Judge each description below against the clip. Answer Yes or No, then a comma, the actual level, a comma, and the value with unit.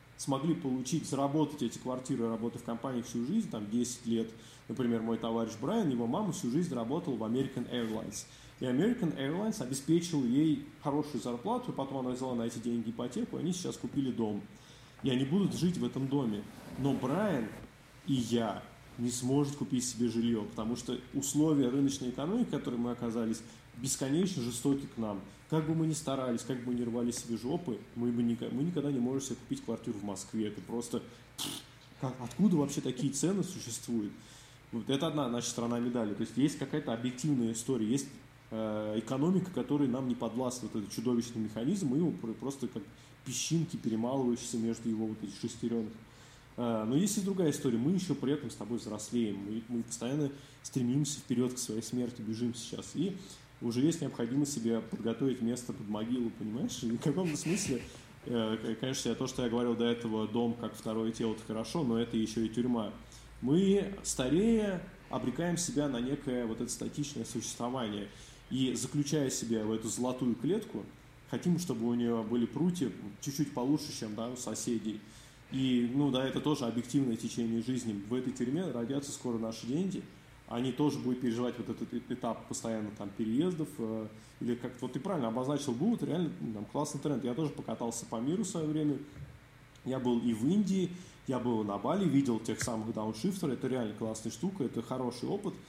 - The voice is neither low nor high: No, low, 125 Hz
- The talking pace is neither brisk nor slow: No, fast, 175 wpm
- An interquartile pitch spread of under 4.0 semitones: Yes, average, 3.3 semitones